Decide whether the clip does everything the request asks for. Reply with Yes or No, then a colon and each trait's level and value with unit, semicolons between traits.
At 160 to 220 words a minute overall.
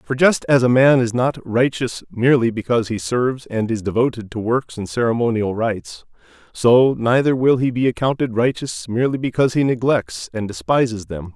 Yes: average, 180 wpm